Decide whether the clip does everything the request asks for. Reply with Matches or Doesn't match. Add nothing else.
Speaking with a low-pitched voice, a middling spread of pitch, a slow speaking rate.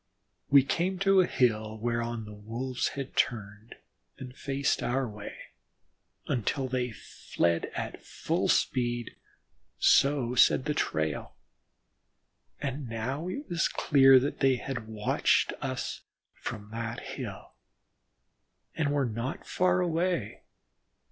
Matches